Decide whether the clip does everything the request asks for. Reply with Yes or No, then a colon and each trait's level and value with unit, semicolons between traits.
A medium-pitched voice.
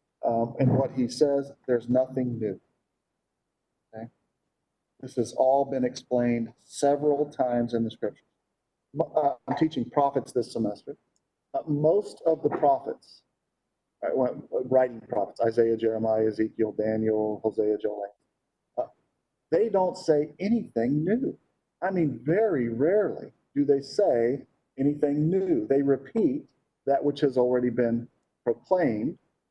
No: low, 130 Hz